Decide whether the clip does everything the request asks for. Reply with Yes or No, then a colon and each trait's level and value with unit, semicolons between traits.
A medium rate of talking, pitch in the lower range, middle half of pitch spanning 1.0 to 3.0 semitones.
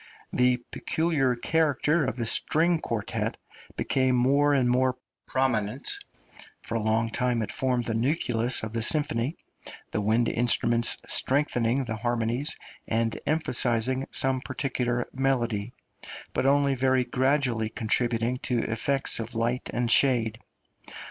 No: slow, 130 wpm; low, 125 Hz; average, 2.7 semitones